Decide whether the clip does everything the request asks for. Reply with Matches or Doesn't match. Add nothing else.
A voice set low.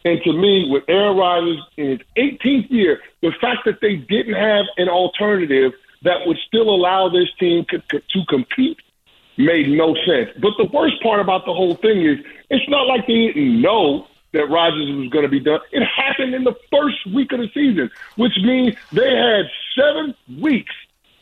Doesn't match